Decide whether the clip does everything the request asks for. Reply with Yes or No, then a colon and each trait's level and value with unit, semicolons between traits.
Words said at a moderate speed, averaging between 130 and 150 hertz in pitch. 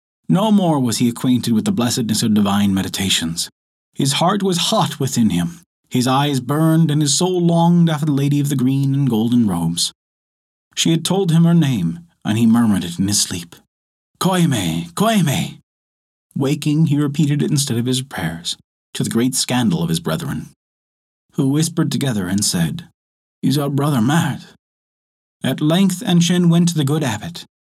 Yes: average, 175 wpm; low, 135 Hz